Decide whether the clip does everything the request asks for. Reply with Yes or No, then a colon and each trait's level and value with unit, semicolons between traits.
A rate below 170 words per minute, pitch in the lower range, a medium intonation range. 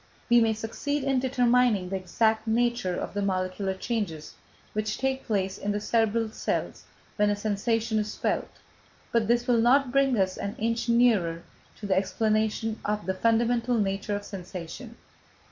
No: average, 160 wpm; high, 220 Hz; average, 3.0 semitones